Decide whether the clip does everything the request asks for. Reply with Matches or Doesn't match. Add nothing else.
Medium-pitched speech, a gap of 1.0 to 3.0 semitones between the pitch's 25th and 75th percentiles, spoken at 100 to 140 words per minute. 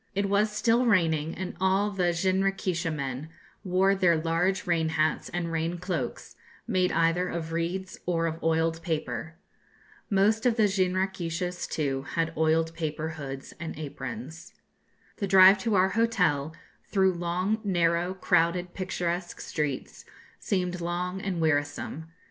Matches